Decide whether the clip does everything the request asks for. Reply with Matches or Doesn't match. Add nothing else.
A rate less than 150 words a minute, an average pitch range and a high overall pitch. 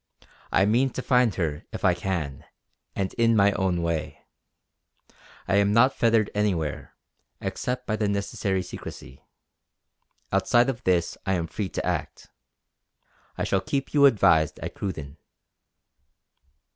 Doesn't match